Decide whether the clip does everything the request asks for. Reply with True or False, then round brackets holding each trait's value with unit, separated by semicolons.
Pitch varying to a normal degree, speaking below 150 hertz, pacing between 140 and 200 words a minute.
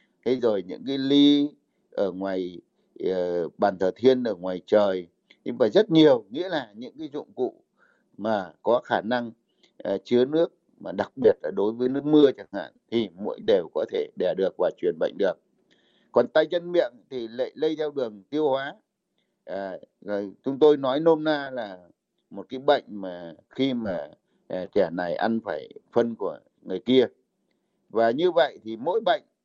False (6.8 semitones; 135 Hz; 185 wpm)